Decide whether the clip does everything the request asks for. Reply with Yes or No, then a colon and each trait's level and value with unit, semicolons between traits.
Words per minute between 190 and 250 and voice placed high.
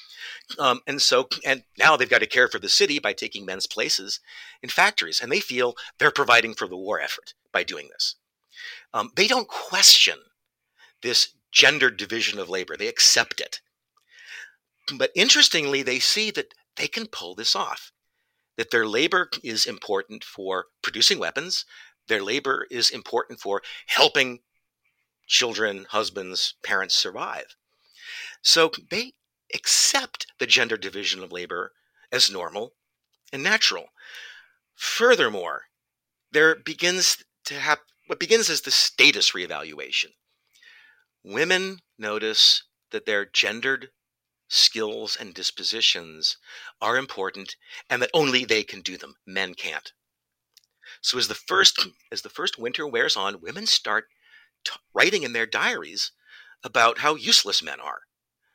No: slow, 135 wpm; very high, 255 Hz